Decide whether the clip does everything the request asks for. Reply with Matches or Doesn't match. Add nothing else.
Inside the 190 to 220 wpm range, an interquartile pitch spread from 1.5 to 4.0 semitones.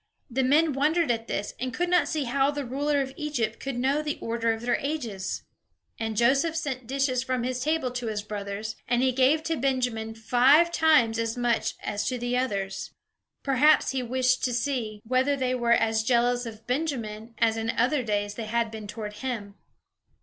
Matches